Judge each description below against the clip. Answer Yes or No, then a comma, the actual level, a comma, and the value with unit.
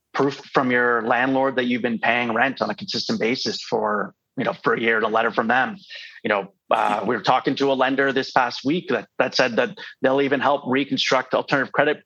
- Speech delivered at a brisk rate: Yes, fast, 225 wpm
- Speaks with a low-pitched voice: Yes, low, 130 Hz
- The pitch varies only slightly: Yes, narrow, 1.8 semitones